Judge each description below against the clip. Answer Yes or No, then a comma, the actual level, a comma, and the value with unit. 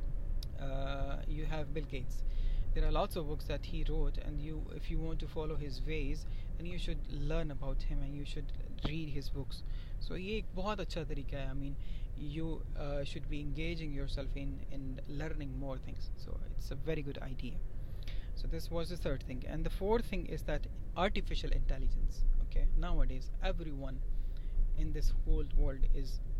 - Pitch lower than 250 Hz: Yes, medium, 140 Hz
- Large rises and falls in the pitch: No, average, 4.3 semitones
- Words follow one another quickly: No, average, 175 wpm